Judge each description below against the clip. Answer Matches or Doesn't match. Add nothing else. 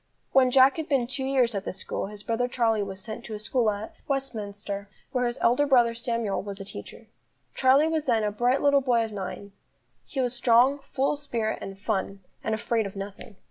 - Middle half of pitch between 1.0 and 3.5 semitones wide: Doesn't match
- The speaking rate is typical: Doesn't match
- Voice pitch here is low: Doesn't match